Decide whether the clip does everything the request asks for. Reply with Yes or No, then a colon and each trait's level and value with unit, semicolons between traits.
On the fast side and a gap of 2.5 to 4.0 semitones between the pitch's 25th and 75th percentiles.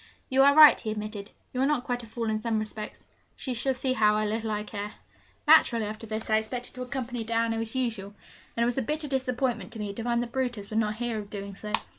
Yes: fast, 245 wpm; average, 2.8 semitones